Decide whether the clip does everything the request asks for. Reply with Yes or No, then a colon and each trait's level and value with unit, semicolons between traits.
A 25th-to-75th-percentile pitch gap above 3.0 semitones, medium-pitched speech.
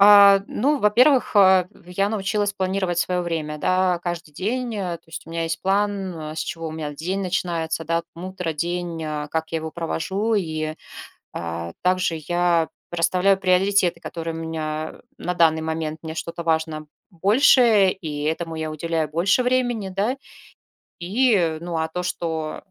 Yes: average, 3.4 semitones; medium, 175 Hz